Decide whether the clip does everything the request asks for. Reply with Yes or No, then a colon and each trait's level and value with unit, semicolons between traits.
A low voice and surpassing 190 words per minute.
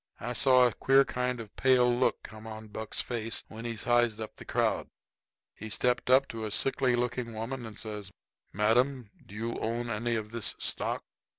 Yes: low, 115 Hz; average, 200 wpm